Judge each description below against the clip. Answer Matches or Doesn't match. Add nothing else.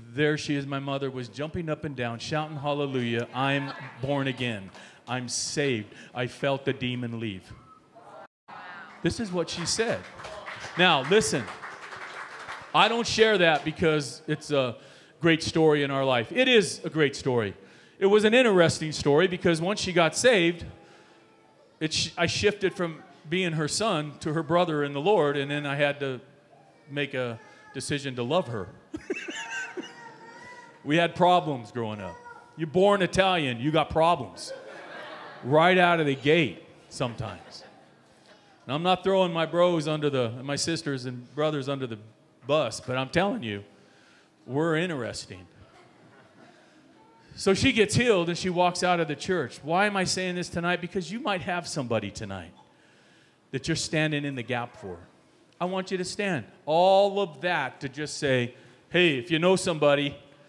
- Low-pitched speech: Doesn't match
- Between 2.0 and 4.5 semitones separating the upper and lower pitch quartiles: Doesn't match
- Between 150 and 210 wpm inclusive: Matches